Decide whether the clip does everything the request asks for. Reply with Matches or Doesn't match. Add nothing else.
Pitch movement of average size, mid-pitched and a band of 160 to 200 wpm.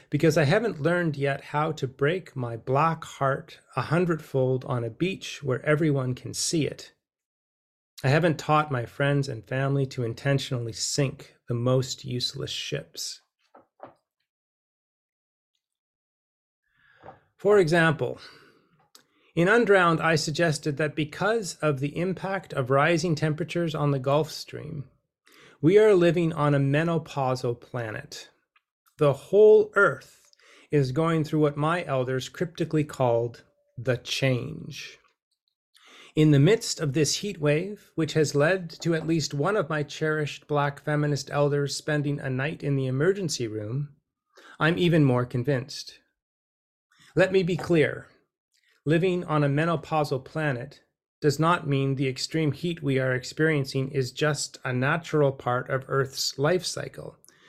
Doesn't match